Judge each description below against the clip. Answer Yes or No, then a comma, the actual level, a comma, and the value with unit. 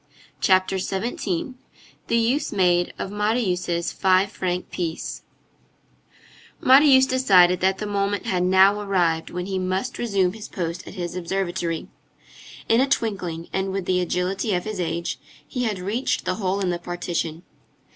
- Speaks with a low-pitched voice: No, high, 190 Hz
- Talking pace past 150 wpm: No, average, 145 wpm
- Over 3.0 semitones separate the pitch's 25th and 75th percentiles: No, average, 2.7 semitones